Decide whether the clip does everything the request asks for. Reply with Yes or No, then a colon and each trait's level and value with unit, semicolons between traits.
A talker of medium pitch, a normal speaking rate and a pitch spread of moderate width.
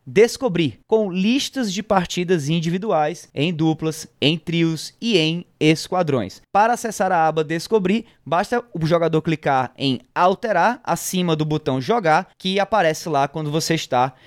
Yes: medium, 165 Hz; average, 145 wpm; average, 3.9 semitones